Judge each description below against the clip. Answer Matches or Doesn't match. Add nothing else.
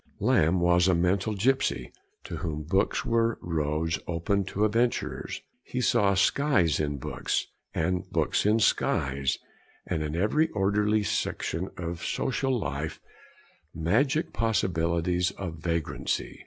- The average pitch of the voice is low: Matches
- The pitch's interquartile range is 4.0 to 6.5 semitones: Matches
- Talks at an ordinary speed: Doesn't match